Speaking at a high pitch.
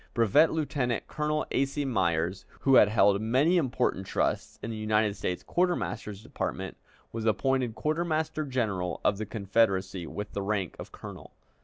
No: low, 110 Hz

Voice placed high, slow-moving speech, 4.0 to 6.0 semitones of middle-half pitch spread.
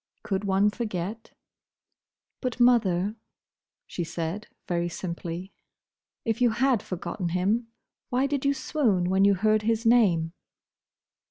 Yes: high, 205 Hz; slow, 120 wpm; average, 4.6 semitones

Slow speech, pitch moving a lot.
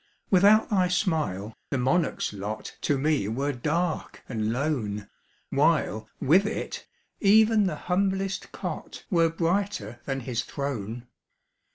Yes: slow, 125 wpm; wide, 7.7 semitones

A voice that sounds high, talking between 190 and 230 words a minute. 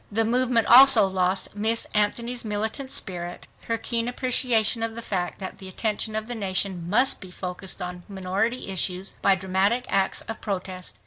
No: high, 205 Hz; average, 170 wpm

